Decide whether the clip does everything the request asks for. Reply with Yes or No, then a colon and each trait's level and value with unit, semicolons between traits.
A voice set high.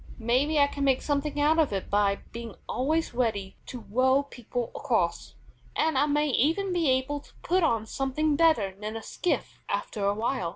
Yes: very high, 265 Hz